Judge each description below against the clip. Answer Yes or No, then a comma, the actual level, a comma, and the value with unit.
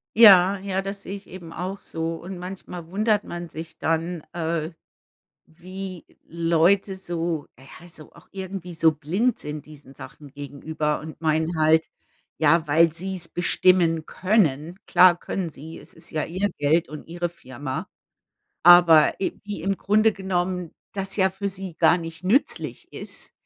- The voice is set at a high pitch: No, medium, 175 Hz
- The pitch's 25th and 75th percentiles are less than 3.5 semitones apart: Yes, average, 3.0 semitones